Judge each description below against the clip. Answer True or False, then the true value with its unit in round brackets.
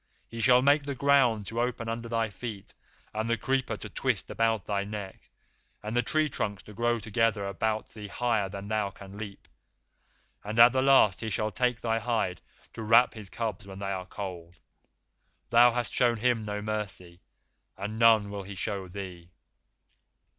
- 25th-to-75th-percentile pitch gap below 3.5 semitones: True (3.0 semitones)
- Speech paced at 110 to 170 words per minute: False (180 wpm)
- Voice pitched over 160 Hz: False (110 Hz)